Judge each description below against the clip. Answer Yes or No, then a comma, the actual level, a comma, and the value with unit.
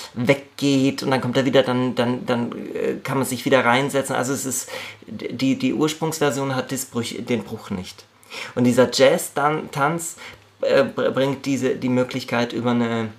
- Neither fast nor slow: Yes, average, 165 wpm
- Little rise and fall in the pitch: Yes, narrow, 1.8 semitones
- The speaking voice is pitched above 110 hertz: Yes, low, 130 Hz